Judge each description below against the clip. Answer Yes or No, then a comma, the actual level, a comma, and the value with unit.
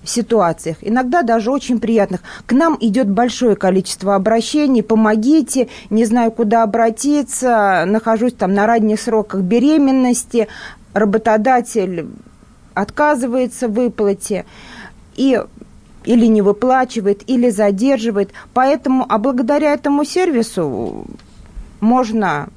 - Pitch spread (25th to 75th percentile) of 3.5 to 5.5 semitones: No, average, 3.1 semitones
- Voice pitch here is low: No, high, 230 Hz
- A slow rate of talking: Yes, slow, 105 wpm